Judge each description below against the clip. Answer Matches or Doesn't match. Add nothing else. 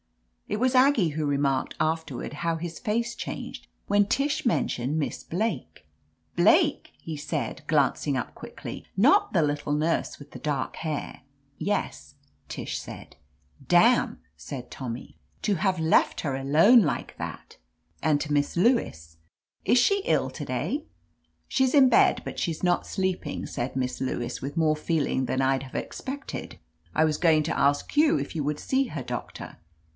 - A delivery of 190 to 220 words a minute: Doesn't match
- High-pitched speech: Doesn't match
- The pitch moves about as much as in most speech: Doesn't match